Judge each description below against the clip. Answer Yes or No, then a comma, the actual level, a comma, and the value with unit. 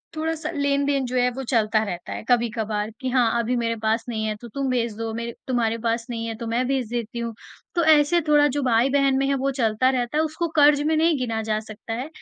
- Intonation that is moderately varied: Yes, average, 3.6 semitones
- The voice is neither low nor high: No, high, 245 Hz